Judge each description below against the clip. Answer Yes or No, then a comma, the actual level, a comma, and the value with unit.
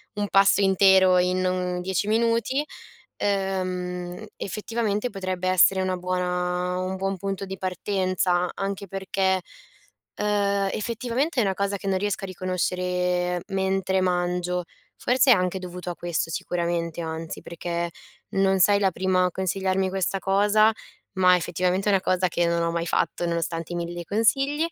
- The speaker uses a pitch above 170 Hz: Yes, medium, 185 Hz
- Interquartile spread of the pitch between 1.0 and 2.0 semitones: Yes, narrow, 1.7 semitones